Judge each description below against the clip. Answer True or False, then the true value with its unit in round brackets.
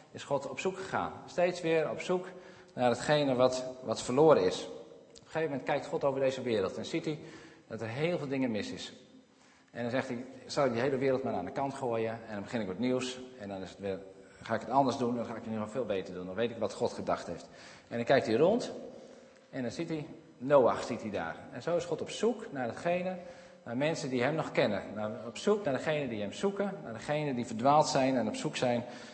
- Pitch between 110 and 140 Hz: True (135 Hz)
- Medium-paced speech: False (255 wpm)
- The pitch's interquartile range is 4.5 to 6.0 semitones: True (5.5 semitones)